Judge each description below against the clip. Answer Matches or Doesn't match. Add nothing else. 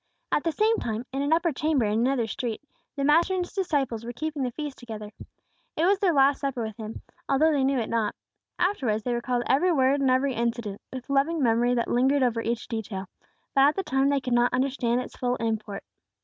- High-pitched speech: Matches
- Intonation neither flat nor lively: Matches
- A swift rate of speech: Matches